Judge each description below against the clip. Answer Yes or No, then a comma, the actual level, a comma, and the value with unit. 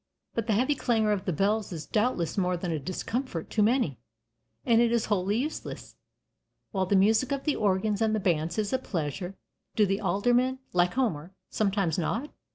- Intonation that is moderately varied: Yes, average, 4.3 semitones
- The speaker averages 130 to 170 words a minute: No, average, 185 wpm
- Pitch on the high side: Yes, high, 205 Hz